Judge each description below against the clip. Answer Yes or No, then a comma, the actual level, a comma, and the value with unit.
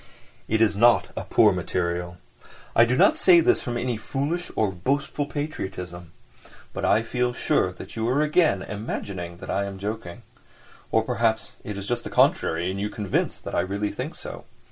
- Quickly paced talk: No, average, 185 wpm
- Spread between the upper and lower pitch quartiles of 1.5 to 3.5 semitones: No, average, 4.7 semitones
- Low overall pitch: Yes, low, 110 Hz